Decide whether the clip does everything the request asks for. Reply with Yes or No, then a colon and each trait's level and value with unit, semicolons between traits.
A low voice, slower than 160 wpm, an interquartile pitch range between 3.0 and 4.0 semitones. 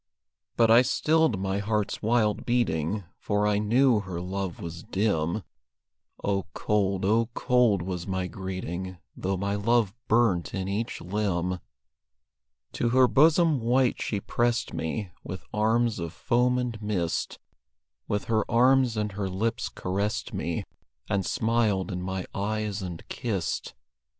Yes: low, 105 Hz; average, 140 wpm; average, 3.7 semitones